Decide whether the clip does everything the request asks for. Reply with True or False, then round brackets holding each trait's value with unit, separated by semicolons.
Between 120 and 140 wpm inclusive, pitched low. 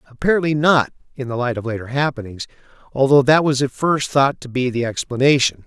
False (190 wpm; 130 Hz)